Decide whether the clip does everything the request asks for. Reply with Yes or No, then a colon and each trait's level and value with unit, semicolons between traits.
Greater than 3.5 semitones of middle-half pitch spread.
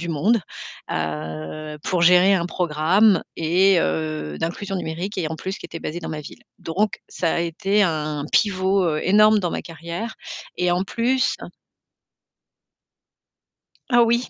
Yes: average, 4.1 semitones